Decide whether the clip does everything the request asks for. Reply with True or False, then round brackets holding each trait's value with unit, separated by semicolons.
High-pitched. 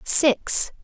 True (260 Hz)